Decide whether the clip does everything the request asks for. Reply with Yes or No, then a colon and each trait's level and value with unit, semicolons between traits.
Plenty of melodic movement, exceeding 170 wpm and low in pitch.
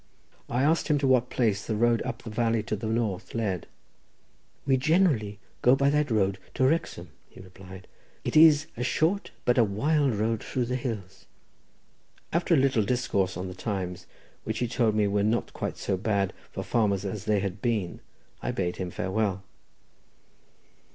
No: average, 4.7 semitones; average, 180 wpm; low, 110 Hz